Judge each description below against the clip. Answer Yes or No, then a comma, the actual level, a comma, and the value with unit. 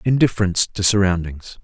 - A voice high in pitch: No, low, 100 Hz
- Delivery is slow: Yes, slow, 110 wpm